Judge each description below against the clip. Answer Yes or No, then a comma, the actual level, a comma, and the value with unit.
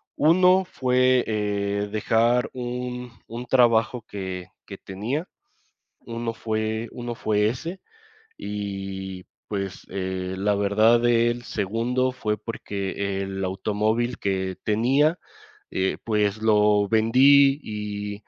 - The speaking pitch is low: Yes, low, 110 Hz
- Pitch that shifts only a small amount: No, average, 3.2 semitones